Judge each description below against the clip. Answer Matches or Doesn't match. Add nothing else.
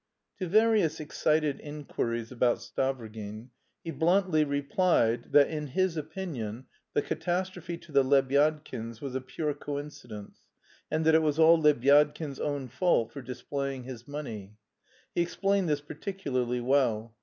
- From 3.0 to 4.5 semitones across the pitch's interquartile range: Matches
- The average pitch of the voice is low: Doesn't match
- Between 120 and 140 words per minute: Matches